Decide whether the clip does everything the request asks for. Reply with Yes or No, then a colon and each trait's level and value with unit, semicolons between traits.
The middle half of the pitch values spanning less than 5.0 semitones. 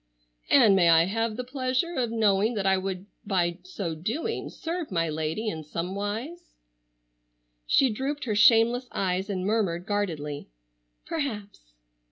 No: average, 5.3 semitones